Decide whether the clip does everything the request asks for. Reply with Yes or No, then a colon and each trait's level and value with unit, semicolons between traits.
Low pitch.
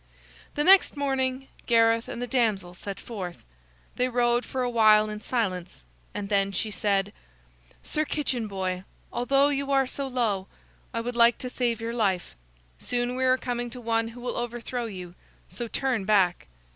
No: high, 235 Hz